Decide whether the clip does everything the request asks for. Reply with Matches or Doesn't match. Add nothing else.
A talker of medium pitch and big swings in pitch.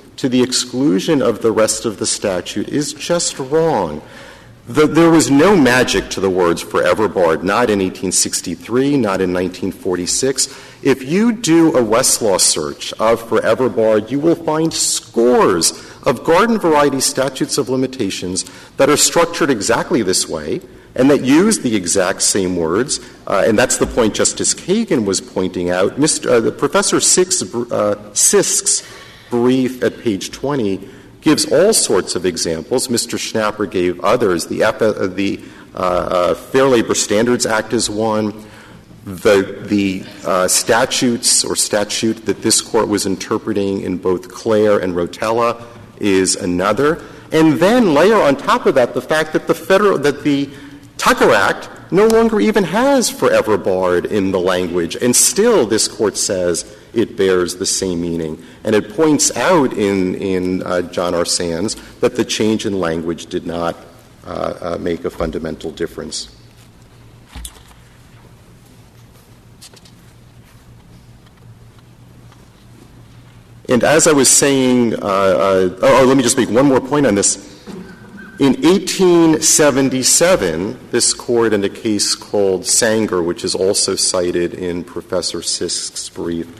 Doesn't match